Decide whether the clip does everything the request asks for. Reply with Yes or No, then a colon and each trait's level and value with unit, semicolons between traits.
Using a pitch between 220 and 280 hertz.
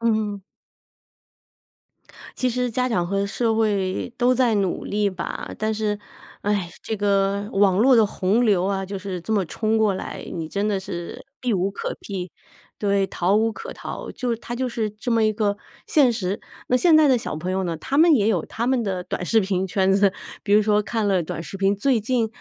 No: high, 205 Hz